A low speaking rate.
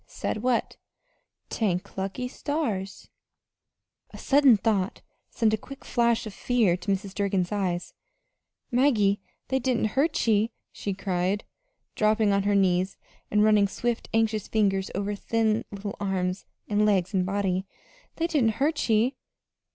No: average, 145 wpm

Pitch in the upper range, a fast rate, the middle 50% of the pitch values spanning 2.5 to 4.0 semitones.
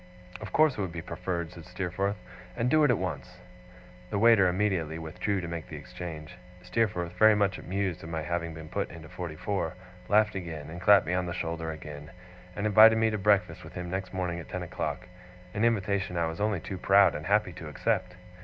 No: very low, 90 Hz; fast, 210 wpm; average, 3.5 semitones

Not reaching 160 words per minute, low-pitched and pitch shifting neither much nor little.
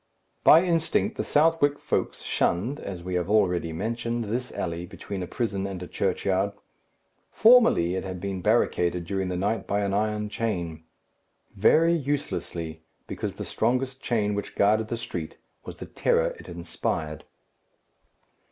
Yes: average, 150 wpm; low, 100 Hz; average, 4.9 semitones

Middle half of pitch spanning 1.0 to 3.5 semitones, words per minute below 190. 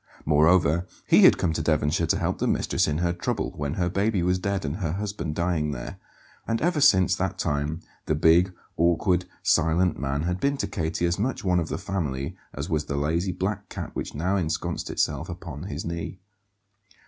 No: average, 3.2 semitones; average, 195 wpm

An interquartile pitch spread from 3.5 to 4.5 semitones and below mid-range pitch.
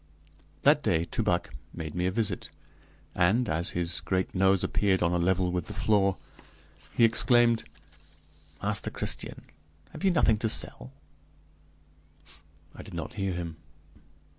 Yes: average, 3.8 semitones; very low, 95 Hz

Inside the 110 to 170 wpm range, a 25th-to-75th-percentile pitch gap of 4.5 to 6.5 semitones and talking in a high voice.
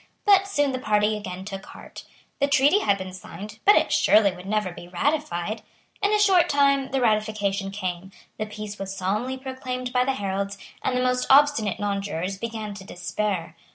No: average, 185 wpm; average, 5.2 semitones; high, 215 Hz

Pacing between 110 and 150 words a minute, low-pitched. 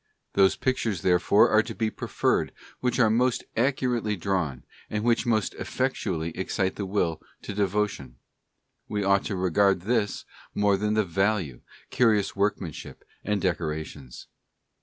Yes: average, 145 wpm; low, 100 Hz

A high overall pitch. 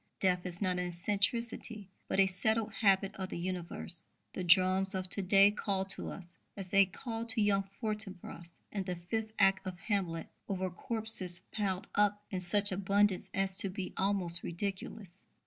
Yes: high, 195 Hz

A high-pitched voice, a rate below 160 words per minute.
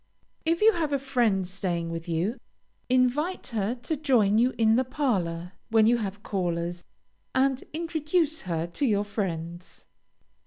Yes: high, 220 Hz; average, 150 wpm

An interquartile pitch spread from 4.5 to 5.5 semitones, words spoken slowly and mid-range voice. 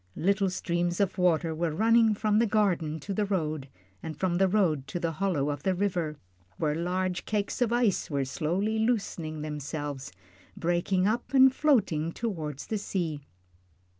No: average, 4.9 semitones; average, 165 wpm; medium, 180 Hz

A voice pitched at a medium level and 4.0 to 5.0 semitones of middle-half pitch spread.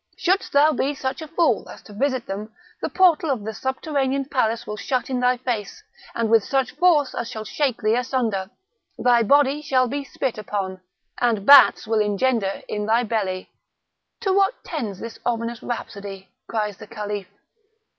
No: high, 240 Hz; average, 4.7 semitones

